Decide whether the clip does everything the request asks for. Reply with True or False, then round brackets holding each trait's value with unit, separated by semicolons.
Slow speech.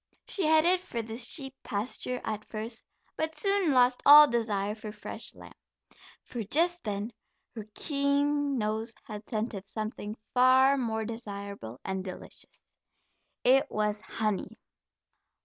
True (130 wpm)